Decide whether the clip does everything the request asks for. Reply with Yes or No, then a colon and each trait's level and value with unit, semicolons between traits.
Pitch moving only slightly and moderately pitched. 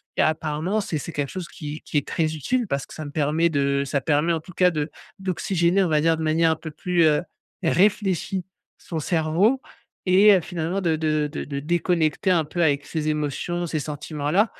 No: average, 3.0 semitones; medium, 160 Hz